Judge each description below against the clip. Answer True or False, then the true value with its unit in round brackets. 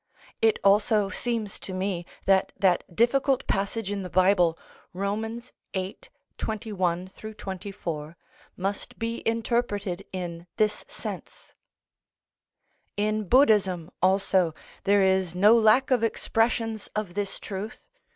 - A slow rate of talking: True (110 wpm)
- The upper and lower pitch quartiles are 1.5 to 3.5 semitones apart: True (2.9 semitones)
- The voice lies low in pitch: False (200 Hz)